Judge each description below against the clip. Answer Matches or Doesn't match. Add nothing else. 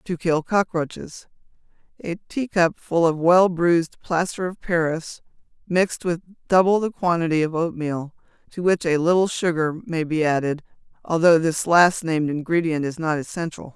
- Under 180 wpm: Matches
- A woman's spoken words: Matches